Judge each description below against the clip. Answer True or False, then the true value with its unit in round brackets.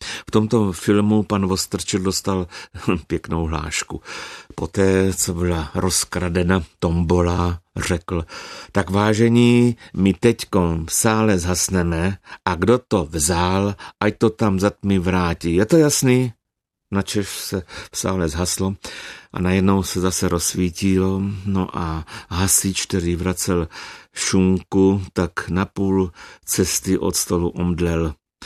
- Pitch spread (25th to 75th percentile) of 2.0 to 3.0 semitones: True (2.5 semitones)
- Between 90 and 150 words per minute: True (120 wpm)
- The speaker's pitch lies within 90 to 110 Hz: True (95 Hz)